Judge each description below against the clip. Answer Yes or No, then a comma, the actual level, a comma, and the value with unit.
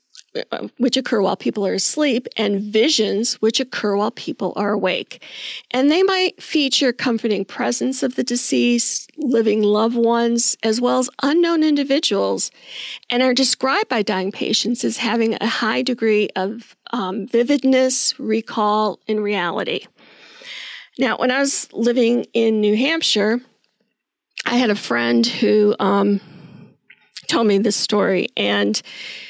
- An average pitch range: Yes, average, 3.6 semitones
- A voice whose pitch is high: Yes, high, 225 Hz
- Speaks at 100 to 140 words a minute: Yes, slow, 135 wpm